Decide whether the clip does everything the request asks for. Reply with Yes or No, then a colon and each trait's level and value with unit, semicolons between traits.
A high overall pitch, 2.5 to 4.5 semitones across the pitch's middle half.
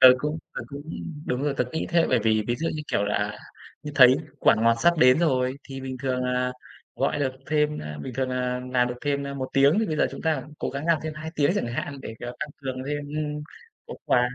No: low, 135 Hz; average, 3.0 semitones